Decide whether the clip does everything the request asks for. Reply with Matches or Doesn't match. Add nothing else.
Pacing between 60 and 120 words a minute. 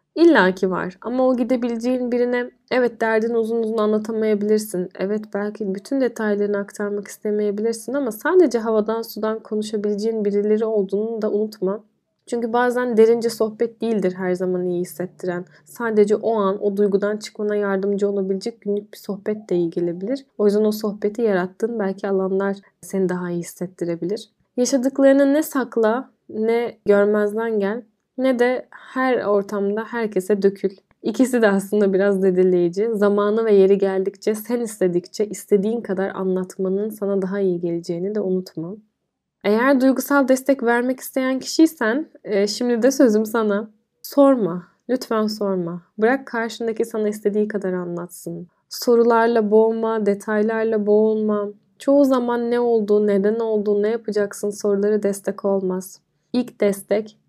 Doesn't match